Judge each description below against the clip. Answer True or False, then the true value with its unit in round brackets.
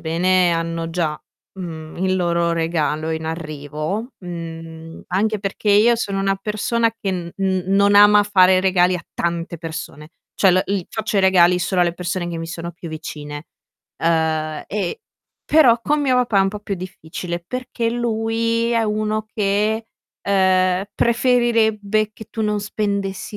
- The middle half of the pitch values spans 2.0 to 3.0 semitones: False (4.0 semitones)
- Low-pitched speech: False (190 Hz)